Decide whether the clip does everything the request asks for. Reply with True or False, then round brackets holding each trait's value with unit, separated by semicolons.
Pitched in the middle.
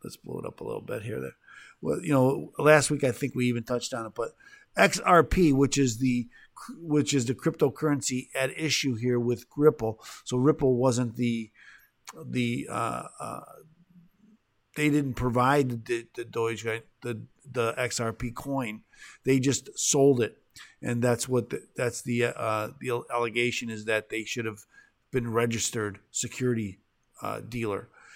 False (125 Hz)